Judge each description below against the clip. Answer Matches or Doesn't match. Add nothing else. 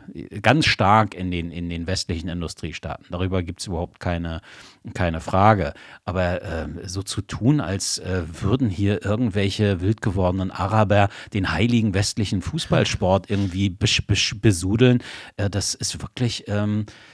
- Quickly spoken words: Doesn't match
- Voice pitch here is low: Matches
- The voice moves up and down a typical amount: Matches